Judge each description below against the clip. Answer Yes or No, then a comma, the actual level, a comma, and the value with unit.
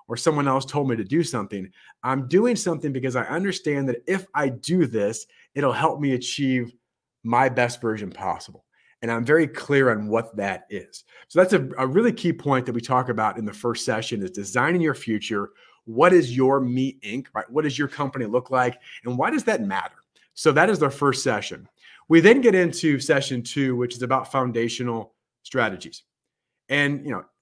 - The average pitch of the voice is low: Yes, low, 130 Hz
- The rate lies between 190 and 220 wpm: Yes, average, 200 wpm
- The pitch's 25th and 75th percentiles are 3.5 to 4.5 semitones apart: Yes, average, 3.8 semitones